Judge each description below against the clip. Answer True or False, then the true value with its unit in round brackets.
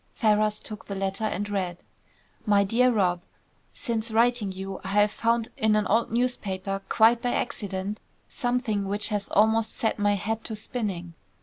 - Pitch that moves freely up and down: False (2.5 semitones)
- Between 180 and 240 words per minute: False (165 wpm)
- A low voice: False (210 Hz)